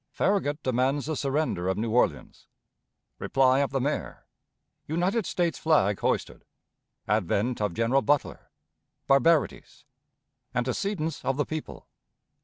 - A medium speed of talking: No, slow, 115 wpm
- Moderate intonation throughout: Yes, average, 4.3 semitones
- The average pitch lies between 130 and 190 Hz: Yes, medium, 140 Hz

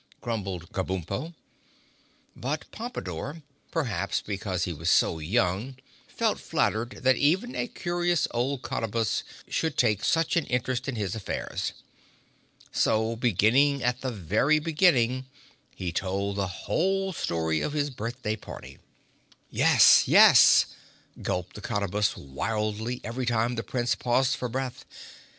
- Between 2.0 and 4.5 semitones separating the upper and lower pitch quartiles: No, average, 5.3 semitones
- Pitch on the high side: No, low, 120 Hz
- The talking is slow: Yes, slow, 130 wpm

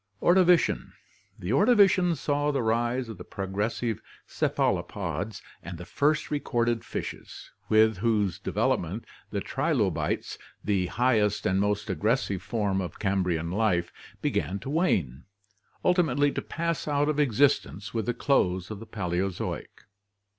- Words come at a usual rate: No, slow, 130 wpm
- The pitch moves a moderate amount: No, wide, 6.8 semitones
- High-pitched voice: No, low, 110 Hz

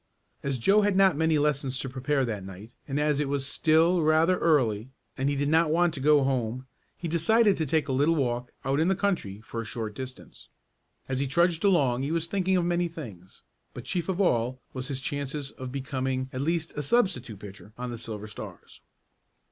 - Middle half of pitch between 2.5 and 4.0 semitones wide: No, average, 4.7 semitones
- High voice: No, medium, 140 Hz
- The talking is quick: Yes, fast, 210 wpm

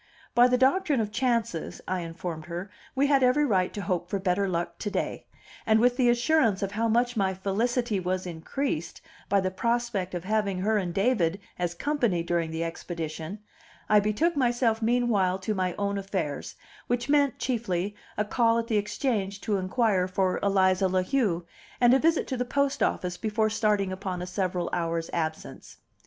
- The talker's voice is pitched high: Yes, high, 200 Hz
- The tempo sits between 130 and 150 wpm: No, average, 180 wpm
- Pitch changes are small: No, average, 4.7 semitones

